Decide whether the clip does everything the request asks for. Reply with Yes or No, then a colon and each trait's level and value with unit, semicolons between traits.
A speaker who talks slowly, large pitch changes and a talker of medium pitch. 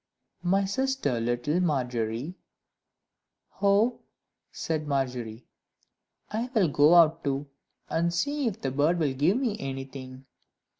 Yes: slow, 115 wpm; wide, 6.7 semitones; medium, 150 Hz